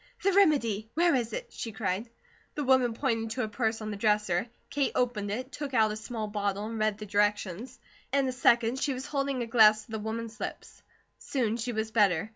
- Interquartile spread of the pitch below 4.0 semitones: Yes, average, 3.3 semitones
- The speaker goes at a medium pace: No, fast, 215 wpm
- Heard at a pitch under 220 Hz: No, high, 225 Hz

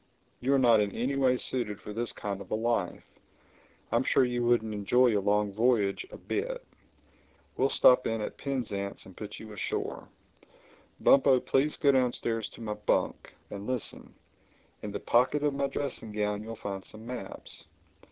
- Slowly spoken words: No, average, 170 wpm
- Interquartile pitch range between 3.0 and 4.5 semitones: Yes, average, 3.6 semitones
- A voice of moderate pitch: No, low, 115 Hz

